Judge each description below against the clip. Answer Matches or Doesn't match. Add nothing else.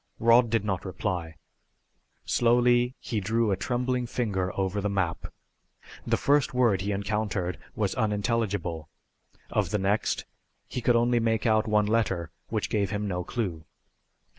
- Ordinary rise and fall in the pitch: Matches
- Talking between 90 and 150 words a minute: Matches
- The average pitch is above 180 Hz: Doesn't match